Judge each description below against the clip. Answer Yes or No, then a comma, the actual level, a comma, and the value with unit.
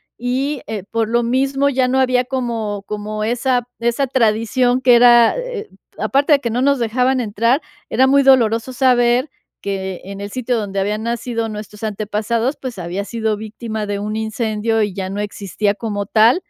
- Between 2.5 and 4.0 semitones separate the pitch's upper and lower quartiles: Yes, average, 3.2 semitones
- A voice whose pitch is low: No, high, 230 Hz